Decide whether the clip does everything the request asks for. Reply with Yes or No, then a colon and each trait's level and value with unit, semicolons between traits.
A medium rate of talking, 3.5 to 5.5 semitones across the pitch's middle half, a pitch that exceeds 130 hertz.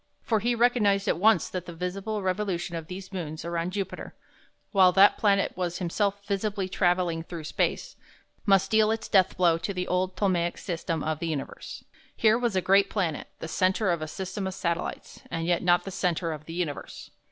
No: average, 195 wpm; average, 2.8 semitones; medium, 185 Hz